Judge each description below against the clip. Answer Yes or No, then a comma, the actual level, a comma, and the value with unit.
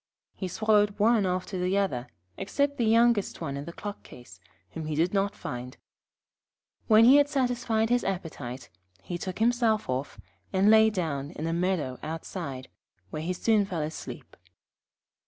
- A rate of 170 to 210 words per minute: No, average, 160 wpm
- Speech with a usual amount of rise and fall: No, wide, 5.9 semitones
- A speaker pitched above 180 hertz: Yes, high, 190 Hz